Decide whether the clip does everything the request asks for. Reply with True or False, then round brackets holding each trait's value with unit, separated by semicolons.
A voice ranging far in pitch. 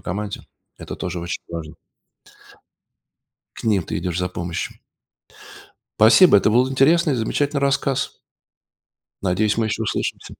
True (7.1 semitones)